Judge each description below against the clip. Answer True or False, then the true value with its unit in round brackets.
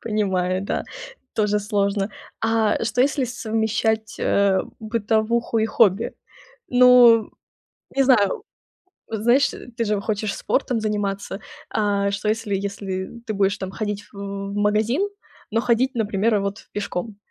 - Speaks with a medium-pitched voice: False (215 Hz)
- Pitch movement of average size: False (2.3 semitones)